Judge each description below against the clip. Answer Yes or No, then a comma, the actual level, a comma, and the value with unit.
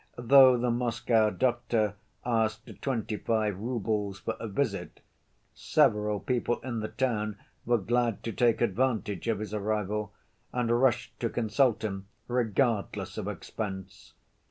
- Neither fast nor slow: No, slow, 130 wpm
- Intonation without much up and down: Yes, narrow, 2.3 semitones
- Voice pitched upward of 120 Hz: No, low, 110 Hz